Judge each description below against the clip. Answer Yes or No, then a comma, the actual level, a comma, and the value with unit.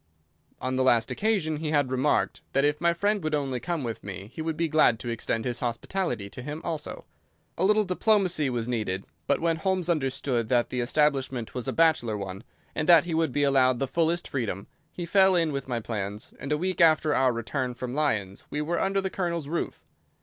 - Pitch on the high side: No, medium, 145 Hz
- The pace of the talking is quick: Yes, fast, 215 wpm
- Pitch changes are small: No, wide, 5.6 semitones